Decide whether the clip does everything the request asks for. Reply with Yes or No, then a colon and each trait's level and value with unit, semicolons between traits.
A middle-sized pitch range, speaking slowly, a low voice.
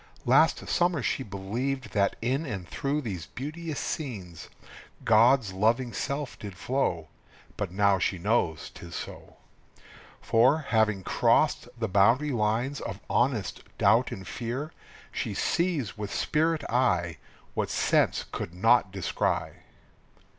No: wide, 5.8 semitones; slow, 130 wpm; low, 115 Hz